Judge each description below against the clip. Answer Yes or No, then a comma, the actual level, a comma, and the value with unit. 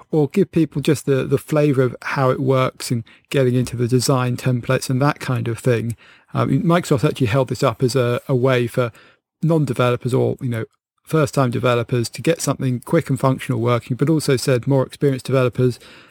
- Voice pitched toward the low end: Yes, low, 130 Hz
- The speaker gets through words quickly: No, average, 195 wpm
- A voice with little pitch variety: Yes, narrow, 2.3 semitones